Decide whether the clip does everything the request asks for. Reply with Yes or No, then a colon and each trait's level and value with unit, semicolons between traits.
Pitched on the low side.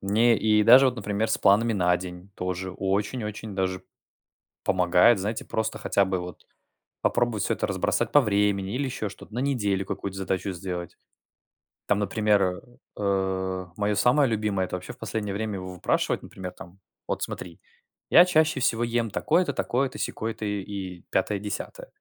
Yes: low, 100 Hz